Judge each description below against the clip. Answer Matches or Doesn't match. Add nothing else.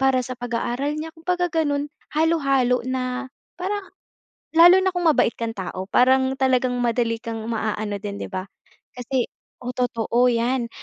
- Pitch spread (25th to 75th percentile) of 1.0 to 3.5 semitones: Doesn't match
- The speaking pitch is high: Matches